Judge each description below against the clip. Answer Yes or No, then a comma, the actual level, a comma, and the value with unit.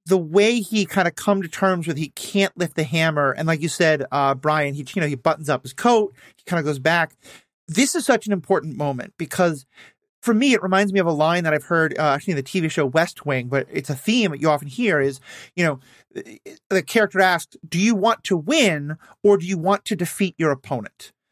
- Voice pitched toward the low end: No, medium, 170 Hz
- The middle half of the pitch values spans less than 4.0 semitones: No, average, 4.7 semitones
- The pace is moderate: No, fast, 245 wpm